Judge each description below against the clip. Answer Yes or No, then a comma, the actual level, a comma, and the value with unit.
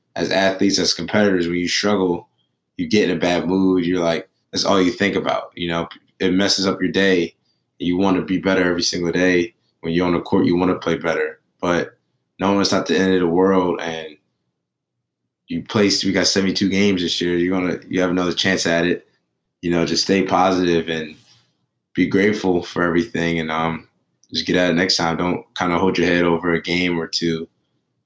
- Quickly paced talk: Yes, fast, 215 wpm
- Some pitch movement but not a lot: No, narrow, 1.9 semitones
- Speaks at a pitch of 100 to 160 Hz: No, very low, 90 Hz